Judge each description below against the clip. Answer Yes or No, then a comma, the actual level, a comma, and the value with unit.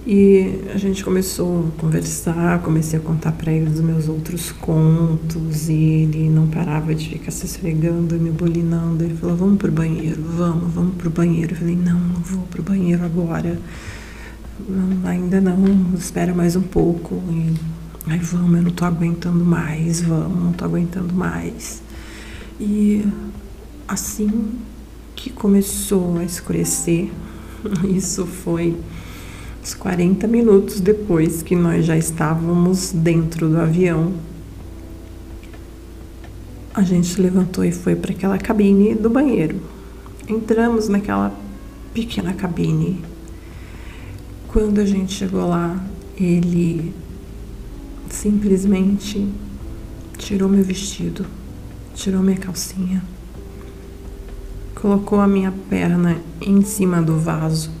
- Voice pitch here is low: No, medium, 170 Hz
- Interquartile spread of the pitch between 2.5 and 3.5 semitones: Yes, average, 3.1 semitones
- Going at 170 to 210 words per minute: No, slow, 120 wpm